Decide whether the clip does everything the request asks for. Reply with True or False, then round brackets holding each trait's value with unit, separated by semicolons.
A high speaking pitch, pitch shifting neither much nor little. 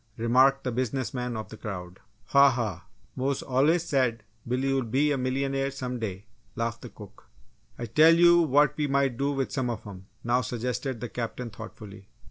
False (125 Hz; 3.1 semitones)